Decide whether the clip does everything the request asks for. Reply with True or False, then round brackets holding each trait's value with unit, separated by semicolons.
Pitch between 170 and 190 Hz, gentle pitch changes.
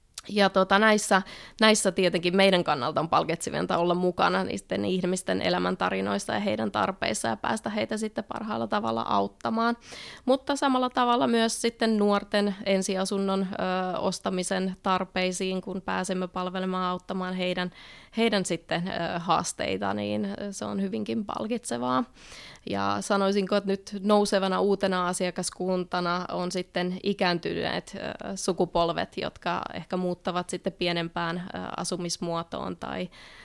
True (185 Hz; 2.2 semitones)